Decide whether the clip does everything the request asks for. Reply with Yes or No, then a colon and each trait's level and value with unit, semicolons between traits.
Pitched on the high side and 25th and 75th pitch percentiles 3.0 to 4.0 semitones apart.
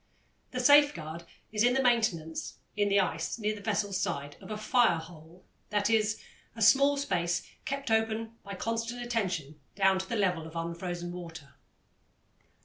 No: high, 200 Hz; average, 5.1 semitones